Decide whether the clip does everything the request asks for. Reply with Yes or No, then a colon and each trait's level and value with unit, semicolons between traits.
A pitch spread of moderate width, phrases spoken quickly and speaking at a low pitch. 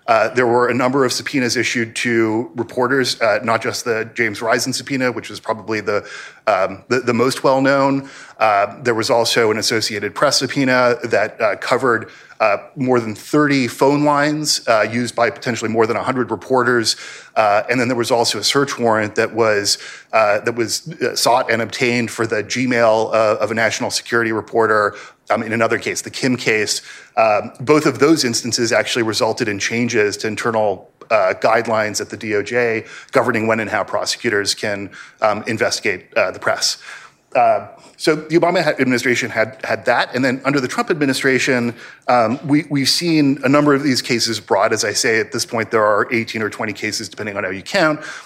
No: average, 3.3 semitones; average, 190 wpm; low, 120 Hz